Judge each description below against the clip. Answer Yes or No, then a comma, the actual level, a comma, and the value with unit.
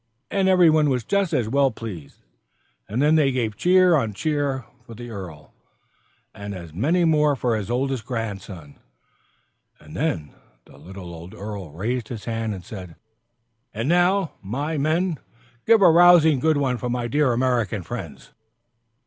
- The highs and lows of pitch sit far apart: Yes, wide, 7.1 semitones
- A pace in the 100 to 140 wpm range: No, average, 160 wpm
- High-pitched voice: No, low, 125 Hz